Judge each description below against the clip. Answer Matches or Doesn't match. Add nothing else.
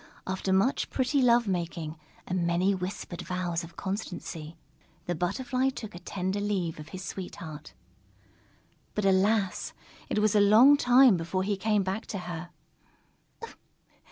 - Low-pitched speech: Doesn't match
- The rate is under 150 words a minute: Matches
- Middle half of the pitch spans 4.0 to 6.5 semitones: Doesn't match